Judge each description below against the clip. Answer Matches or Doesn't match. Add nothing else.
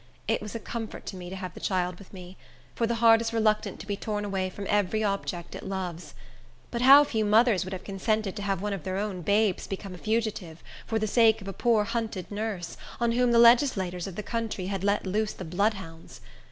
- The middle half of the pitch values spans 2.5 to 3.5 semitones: Matches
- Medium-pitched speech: Doesn't match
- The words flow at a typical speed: Doesn't match